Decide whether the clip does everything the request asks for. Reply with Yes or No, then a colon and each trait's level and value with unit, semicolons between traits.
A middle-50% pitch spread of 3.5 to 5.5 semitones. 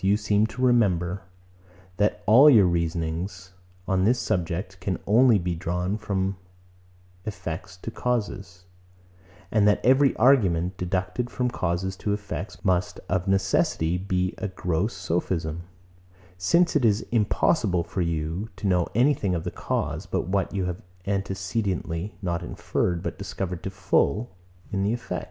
No: average, 3.1 semitones